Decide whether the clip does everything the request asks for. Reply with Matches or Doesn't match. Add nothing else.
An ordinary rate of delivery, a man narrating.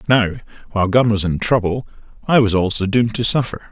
Matches